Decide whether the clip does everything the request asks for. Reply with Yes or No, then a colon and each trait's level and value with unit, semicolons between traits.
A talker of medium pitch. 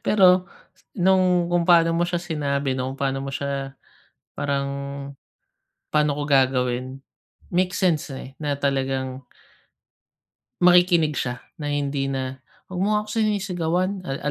Yes: medium, 145 Hz